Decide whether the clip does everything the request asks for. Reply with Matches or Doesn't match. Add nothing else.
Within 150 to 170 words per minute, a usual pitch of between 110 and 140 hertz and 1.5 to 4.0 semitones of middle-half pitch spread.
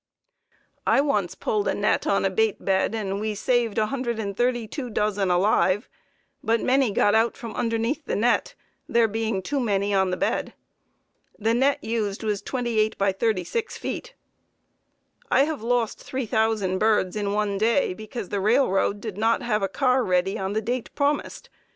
Doesn't match